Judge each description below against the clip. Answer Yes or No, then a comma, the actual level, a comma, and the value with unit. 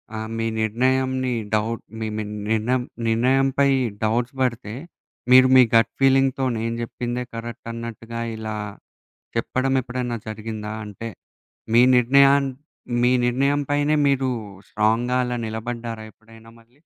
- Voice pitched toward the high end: No, low, 120 Hz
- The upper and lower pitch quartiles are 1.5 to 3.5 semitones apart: Yes, narrow, 2.5 semitones